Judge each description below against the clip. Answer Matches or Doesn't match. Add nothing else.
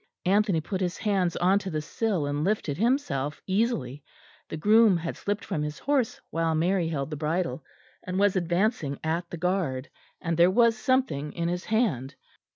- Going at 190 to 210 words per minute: Doesn't match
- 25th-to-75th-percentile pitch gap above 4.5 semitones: Matches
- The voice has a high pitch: Doesn't match